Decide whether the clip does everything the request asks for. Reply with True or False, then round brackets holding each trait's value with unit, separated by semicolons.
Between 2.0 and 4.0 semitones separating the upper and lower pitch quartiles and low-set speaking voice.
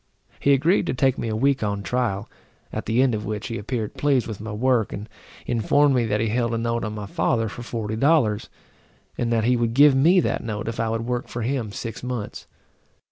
True (3.0 semitones; 115 Hz)